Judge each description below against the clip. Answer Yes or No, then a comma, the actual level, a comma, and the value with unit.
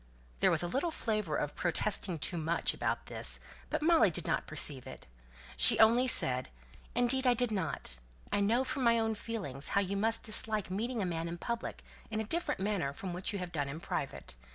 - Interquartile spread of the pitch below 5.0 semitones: No, wide, 5.4 semitones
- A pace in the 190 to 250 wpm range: Yes, fast, 205 wpm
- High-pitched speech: Yes, high, 205 Hz